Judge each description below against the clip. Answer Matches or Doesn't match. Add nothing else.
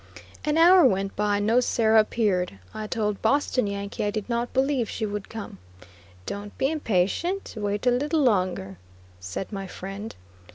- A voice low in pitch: Doesn't match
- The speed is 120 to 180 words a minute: Matches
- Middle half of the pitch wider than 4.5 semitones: Doesn't match